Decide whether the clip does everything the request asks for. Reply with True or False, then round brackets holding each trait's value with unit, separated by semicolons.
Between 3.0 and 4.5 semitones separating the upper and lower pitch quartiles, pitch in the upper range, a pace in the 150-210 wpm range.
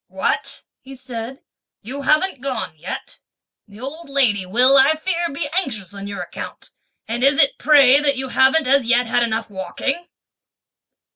True (3.8 semitones; 265 Hz; 160 wpm)